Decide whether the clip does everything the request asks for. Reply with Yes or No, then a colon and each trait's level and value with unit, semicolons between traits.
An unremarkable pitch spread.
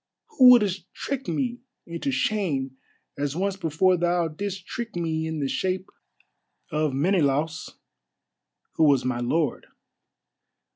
Yes: average, 4.8 semitones